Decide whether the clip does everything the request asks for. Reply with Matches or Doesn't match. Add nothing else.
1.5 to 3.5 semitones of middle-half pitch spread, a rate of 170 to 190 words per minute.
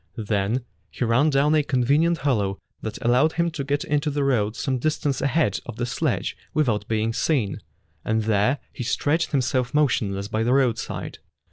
Doesn't match